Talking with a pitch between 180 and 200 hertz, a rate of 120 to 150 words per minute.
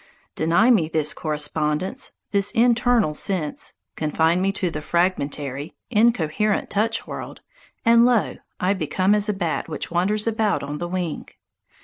Yes: medium, 185 Hz; average, 140 wpm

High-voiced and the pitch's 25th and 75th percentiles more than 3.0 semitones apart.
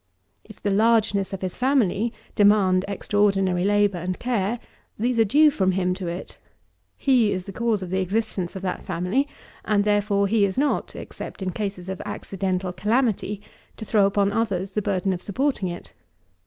No: high, 200 Hz; average, 2.7 semitones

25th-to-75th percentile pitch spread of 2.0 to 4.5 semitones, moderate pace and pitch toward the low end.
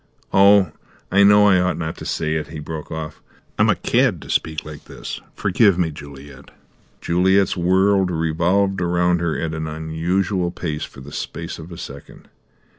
Yes: average, 3.1 semitones; average, 175 wpm; very low, 85 Hz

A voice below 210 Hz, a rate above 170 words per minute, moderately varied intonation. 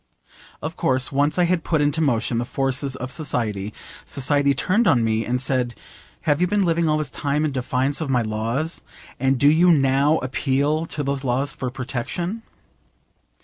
Yes: medium, 140 Hz; average, 180 wpm; average, 3.5 semitones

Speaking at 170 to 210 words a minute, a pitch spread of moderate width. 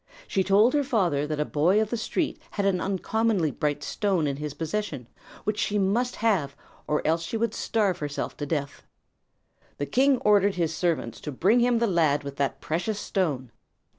No: average, 195 wpm; wide, 6.1 semitones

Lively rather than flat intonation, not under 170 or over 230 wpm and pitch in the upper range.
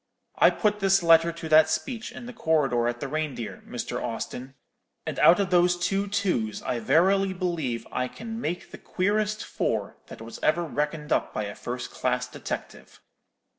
No: wide, 6.6 semitones; average, 175 wpm; medium, 165 Hz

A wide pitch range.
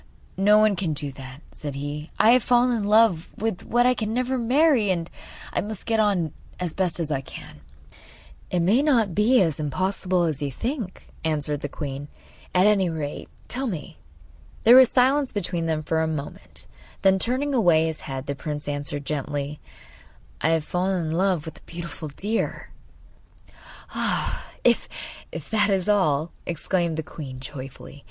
Yes: wide, 6.2 semitones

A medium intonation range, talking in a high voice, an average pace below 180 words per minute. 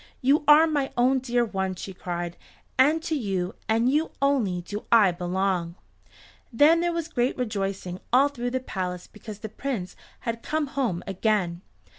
No: wide, 6.6 semitones; high, 230 Hz; average, 165 wpm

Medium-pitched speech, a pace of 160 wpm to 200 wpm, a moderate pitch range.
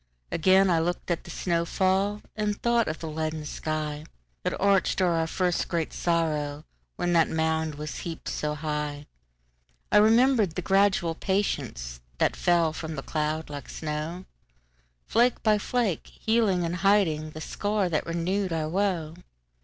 No: medium, 165 Hz; slow, 135 wpm; average, 4.0 semitones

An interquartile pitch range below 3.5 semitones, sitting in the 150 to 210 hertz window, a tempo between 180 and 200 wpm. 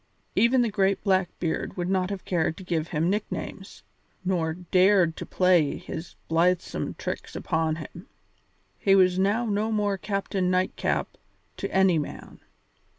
No: average, 2.7 semitones; medium, 185 Hz; average, 145 wpm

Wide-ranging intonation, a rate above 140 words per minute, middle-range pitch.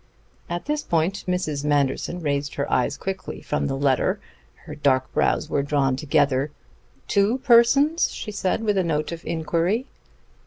Yes: wide, 5.8 semitones; average, 155 wpm; medium, 160 Hz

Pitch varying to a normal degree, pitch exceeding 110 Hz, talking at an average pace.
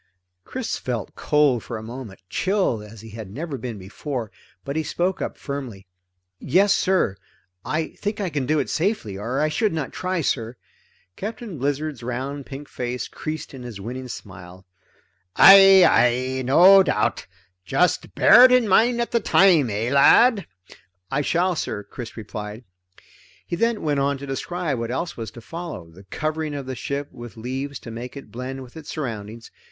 No: wide, 6.6 semitones; medium, 140 Hz; average, 175 wpm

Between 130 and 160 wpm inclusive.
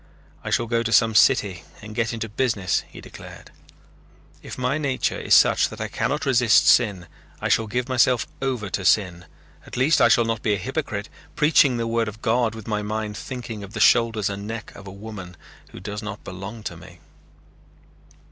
No: average, 195 wpm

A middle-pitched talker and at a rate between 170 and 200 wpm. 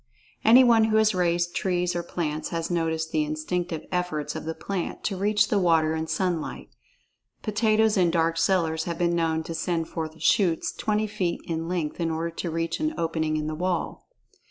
Yes: medium, 170 Hz; average, 185 wpm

